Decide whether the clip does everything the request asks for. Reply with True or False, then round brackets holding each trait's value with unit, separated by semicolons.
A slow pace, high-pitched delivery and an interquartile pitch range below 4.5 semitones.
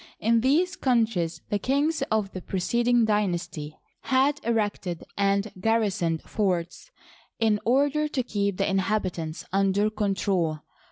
True (120 wpm; 210 Hz; 4.1 semitones)